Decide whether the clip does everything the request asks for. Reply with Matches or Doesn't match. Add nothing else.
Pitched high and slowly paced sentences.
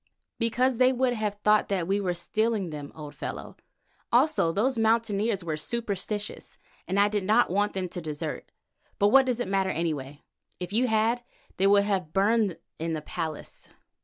Doesn't match